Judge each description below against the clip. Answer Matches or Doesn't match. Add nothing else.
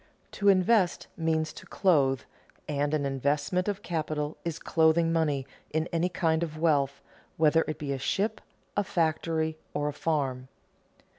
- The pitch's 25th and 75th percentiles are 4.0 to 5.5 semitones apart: Doesn't match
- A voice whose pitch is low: Doesn't match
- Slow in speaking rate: Doesn't match